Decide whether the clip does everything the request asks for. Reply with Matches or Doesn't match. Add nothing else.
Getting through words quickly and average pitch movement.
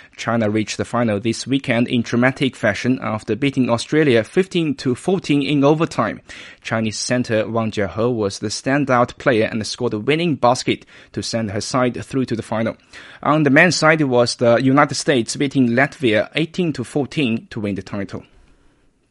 Doesn't match